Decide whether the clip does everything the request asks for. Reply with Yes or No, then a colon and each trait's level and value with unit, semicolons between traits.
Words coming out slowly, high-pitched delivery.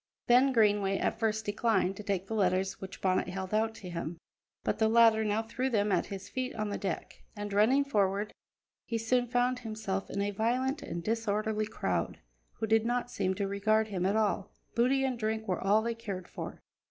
No: average, 200 wpm; high, 215 Hz